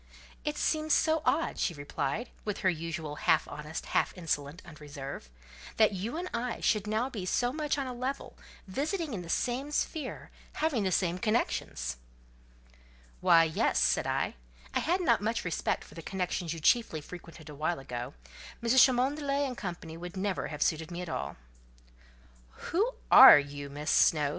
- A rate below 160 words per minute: No, average, 165 wpm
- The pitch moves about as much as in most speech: No, wide, 8.3 semitones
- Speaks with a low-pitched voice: No, high, 190 Hz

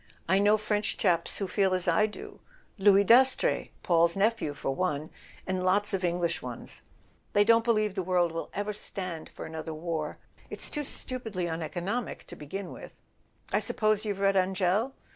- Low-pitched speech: No, high, 195 Hz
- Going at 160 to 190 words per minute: Yes, average, 170 wpm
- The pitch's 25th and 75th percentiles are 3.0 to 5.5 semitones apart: Yes, average, 3.6 semitones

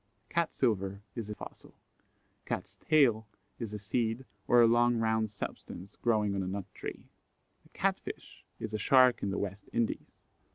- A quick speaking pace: No, average, 170 wpm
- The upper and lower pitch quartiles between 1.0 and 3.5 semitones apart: Yes, average, 3.0 semitones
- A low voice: Yes, low, 110 Hz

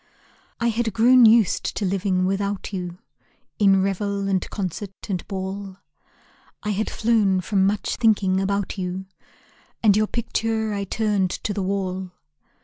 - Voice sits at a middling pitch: No, high, 200 Hz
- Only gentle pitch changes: Yes, narrow, 2.1 semitones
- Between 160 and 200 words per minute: No, average, 140 wpm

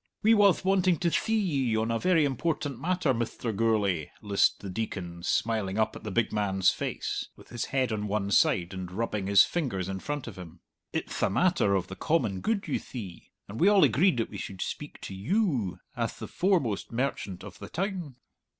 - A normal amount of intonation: No, wide, 8.9 semitones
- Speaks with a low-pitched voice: Yes, low, 115 Hz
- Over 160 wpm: Yes, fast, 205 wpm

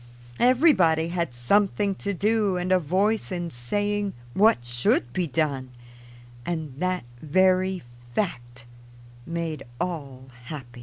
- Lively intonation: Yes, wide, 6.3 semitones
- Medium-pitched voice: Yes, medium, 175 Hz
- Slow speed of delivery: Yes, slow, 115 wpm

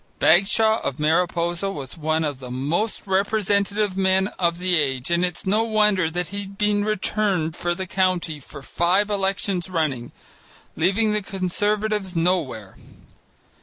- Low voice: No, medium, 185 Hz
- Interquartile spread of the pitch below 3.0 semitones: No, average, 3.9 semitones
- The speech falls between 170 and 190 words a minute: No, average, 145 wpm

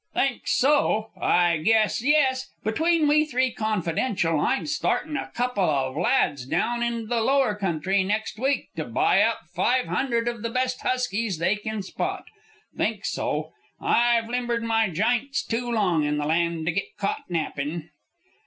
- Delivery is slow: No, average, 160 wpm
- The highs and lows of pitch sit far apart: Yes, wide, 6.3 semitones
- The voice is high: Yes, high, 225 Hz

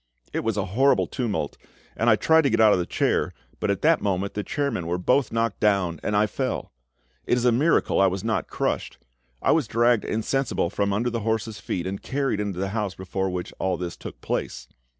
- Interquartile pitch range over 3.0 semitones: Yes, average, 3.7 semitones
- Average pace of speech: No, fast, 220 wpm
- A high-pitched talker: No, low, 105 Hz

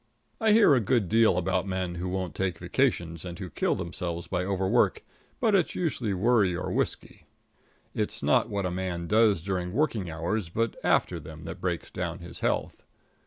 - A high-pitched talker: No, very low, 95 Hz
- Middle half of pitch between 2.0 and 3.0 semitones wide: No, average, 4.2 semitones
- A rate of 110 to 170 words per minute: No, average, 180 wpm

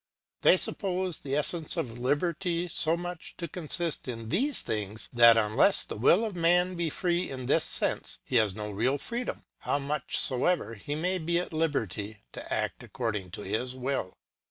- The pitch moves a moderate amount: No, wide, 7.1 semitones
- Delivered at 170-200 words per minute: Yes, average, 180 wpm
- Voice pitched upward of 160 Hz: No, medium, 145 Hz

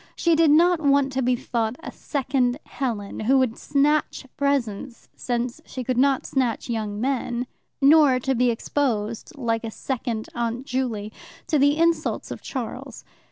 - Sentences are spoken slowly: No, average, 160 wpm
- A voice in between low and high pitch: No, very high, 255 Hz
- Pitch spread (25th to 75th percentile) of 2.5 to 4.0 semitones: Yes, average, 3.2 semitones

